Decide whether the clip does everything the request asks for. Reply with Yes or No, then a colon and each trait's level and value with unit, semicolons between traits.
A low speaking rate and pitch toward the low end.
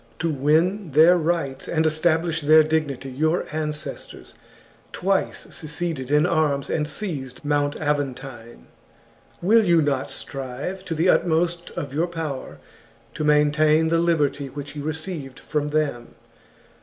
No: slow, 130 wpm; medium, 155 Hz